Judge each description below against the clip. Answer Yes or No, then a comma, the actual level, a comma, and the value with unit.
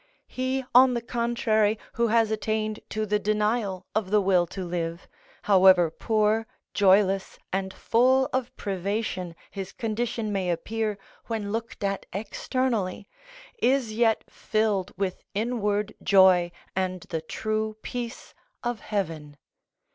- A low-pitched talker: No, high, 210 Hz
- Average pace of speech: No, slow, 125 wpm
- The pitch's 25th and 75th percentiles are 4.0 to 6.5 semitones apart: No, average, 3.1 semitones